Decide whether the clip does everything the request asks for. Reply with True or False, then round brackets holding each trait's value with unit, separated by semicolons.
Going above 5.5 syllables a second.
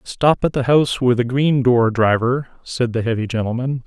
False (5.0 syllables/s)